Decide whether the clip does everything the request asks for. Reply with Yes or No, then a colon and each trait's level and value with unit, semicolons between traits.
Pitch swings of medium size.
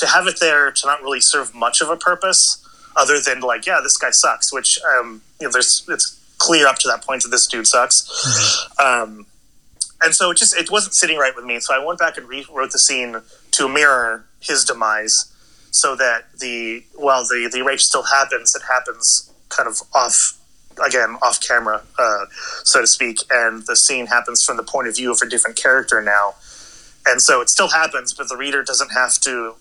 No: wide, 6.2 semitones